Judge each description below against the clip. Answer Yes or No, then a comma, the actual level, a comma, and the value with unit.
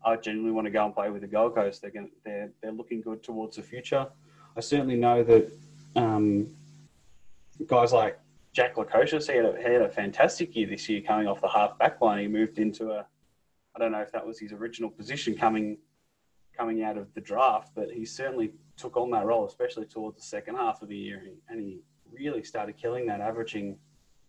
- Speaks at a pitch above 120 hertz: No, low, 110 Hz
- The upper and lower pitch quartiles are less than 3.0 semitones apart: No, average, 4.1 semitones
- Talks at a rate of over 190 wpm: Yes, fast, 205 wpm